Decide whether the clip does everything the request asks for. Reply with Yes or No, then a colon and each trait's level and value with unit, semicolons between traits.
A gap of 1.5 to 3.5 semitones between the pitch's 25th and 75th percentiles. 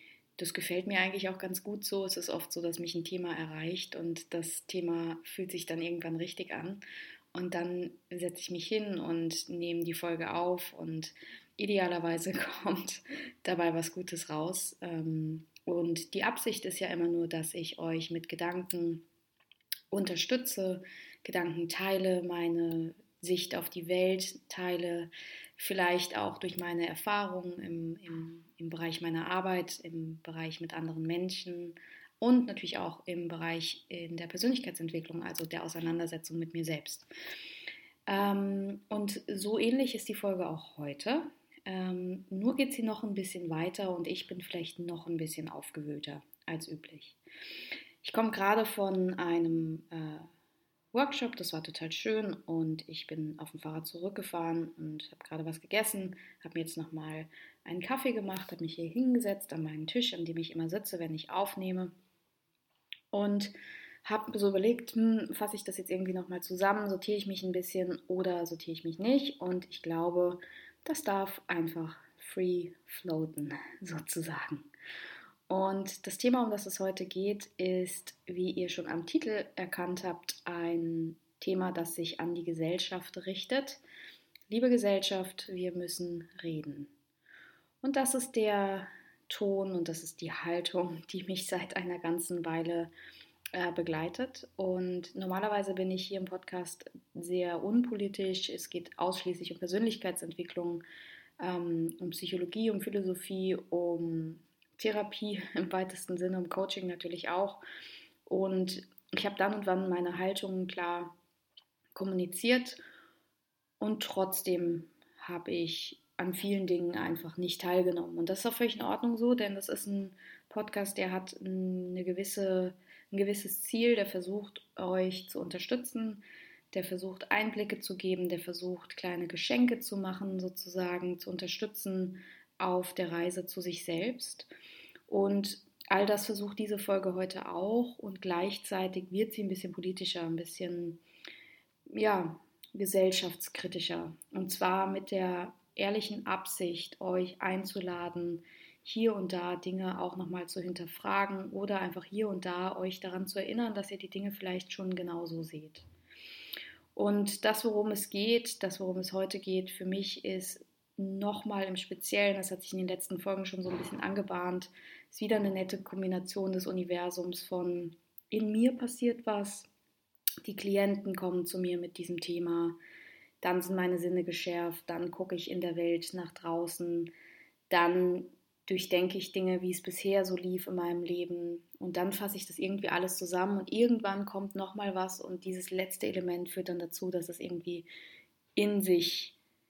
Yes: narrow, 2.5 semitones